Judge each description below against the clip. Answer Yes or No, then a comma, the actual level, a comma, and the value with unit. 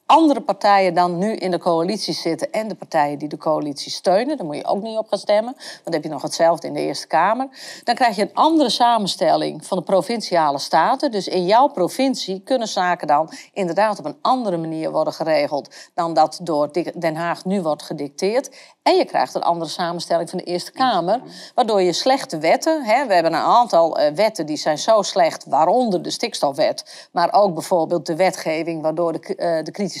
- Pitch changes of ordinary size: No, wide, 6.1 semitones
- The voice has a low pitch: No, medium, 185 Hz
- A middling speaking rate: No, fast, 205 wpm